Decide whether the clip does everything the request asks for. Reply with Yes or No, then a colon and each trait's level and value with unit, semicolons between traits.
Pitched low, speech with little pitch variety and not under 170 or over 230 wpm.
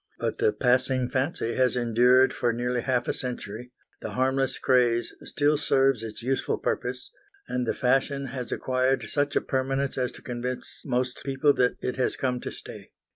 Yes: low, 130 Hz; narrow, 1.5 semitones; average, 175 wpm